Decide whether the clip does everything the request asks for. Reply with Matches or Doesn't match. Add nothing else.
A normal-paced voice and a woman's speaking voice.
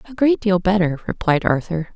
Matches